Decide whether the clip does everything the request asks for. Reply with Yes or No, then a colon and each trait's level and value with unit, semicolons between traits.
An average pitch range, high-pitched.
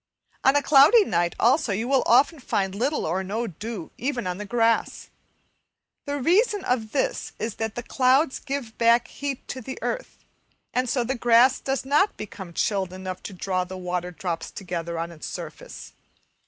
No: wide, 6.2 semitones; high, 230 Hz